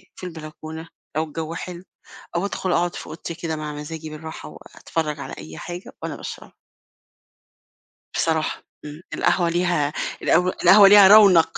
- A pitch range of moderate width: No, narrow, 2.3 semitones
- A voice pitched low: No, medium, 165 Hz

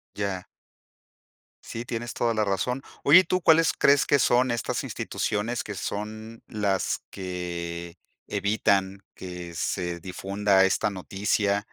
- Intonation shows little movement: No, average, 3.8 semitones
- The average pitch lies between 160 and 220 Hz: No, low, 100 Hz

